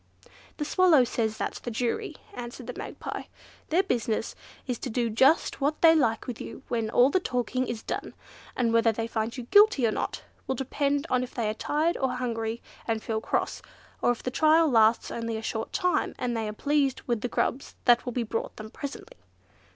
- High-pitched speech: Yes, high, 245 Hz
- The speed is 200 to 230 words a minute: Yes, fast, 205 wpm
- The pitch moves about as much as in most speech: Yes, average, 3.7 semitones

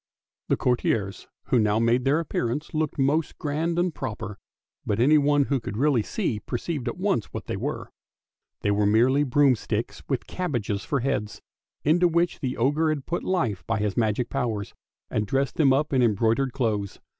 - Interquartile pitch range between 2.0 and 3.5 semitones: No, average, 5.3 semitones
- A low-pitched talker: Yes, low, 130 Hz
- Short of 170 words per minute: No, average, 175 wpm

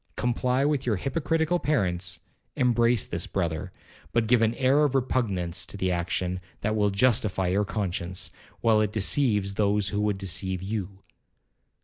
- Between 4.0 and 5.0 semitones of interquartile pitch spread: Yes, average, 4.6 semitones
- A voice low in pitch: Yes, low, 105 Hz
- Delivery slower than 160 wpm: Yes, average, 150 wpm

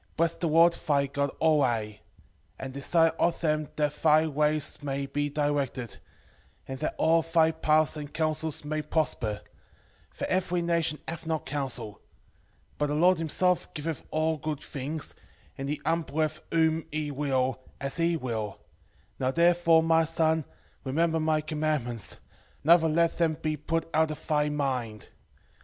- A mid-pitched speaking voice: Yes, medium, 155 Hz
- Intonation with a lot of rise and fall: No, narrow, 2.5 semitones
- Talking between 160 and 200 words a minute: No, average, 150 wpm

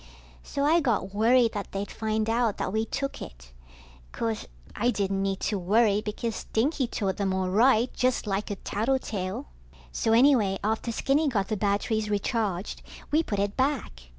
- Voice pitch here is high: Yes, high, 215 Hz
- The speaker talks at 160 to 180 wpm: Yes, average, 170 wpm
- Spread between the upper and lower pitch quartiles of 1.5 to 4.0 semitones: Yes, average, 3.4 semitones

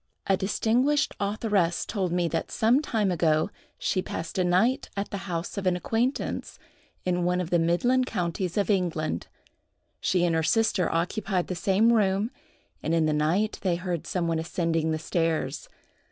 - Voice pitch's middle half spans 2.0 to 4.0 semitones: Yes, average, 3.6 semitones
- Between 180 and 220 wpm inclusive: No, average, 170 wpm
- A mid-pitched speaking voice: Yes, medium, 180 Hz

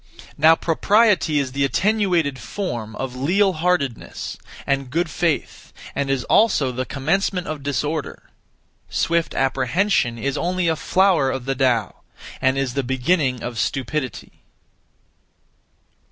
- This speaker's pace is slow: Yes, slow, 125 wpm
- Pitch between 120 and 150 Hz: Yes, medium, 140 Hz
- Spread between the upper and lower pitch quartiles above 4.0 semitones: Yes, average, 5.0 semitones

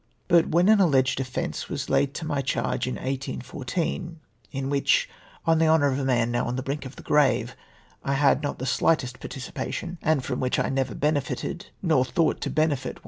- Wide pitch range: No, average, 3.5 semitones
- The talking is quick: Yes, fast, 220 wpm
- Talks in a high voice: No, medium, 140 Hz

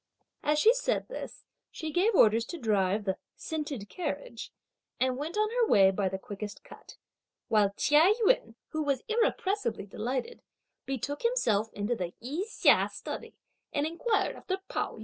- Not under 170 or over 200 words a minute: No, average, 160 wpm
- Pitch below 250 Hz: No, very high, 285 Hz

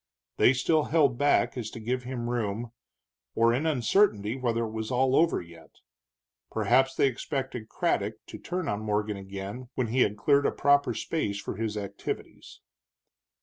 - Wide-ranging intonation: No, average, 3.8 semitones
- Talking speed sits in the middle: Yes, average, 170 wpm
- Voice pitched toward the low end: Yes, low, 120 Hz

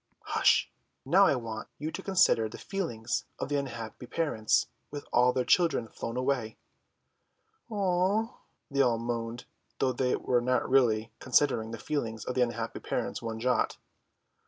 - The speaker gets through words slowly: No, average, 155 wpm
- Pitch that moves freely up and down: No, average, 4.1 semitones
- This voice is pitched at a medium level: No, low, 125 Hz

